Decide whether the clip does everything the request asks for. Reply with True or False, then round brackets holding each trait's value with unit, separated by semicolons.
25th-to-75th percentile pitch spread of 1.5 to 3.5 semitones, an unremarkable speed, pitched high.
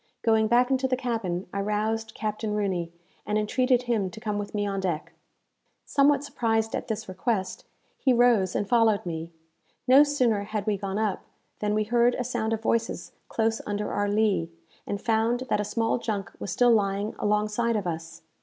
True (2.6 semitones; 185 wpm; 215 Hz)